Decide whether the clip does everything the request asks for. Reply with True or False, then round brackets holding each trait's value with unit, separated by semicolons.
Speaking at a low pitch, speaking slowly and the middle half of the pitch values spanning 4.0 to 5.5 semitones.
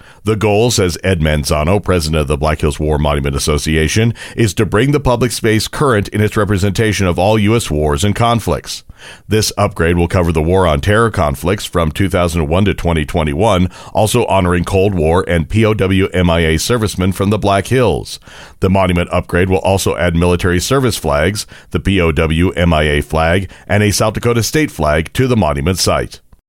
False (95 Hz; 175 wpm; 4.4 semitones)